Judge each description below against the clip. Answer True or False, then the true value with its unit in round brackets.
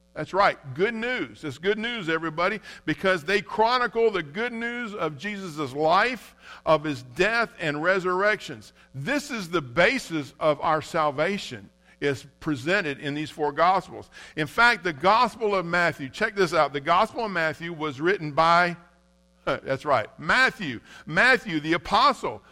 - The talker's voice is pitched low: False (170 Hz)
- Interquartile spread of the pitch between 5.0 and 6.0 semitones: True (5.4 semitones)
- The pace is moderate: True (150 wpm)